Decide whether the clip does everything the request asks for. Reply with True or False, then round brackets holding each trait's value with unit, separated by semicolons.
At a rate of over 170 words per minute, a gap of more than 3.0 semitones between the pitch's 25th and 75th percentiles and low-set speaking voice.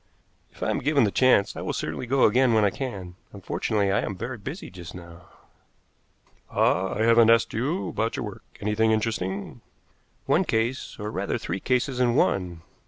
True (180 wpm; 4.4 semitones; 110 Hz)